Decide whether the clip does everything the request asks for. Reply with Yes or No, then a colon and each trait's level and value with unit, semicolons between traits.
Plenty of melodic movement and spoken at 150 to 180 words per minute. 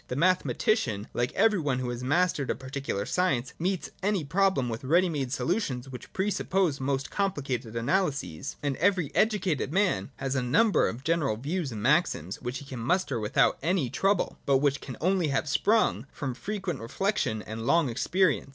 Yes: wide, 6.7 semitones; average, 175 wpm